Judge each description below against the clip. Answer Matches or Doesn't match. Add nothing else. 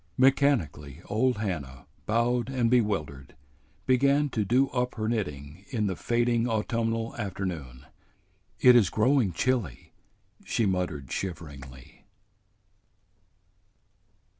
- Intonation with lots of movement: Matches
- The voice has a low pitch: Matches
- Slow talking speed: Matches